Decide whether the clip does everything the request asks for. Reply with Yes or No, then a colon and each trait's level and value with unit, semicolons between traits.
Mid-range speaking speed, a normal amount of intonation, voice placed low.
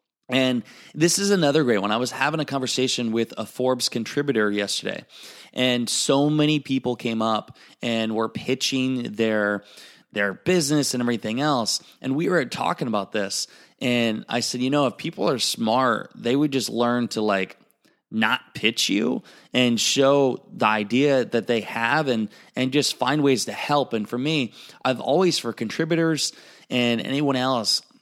Yes: average, 170 wpm; average, 3.5 semitones; low, 125 Hz